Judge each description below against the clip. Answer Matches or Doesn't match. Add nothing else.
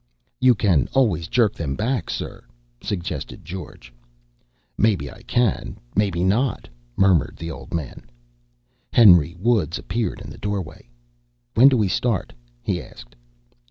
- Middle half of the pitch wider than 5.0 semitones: Matches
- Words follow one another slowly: Matches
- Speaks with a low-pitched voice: Matches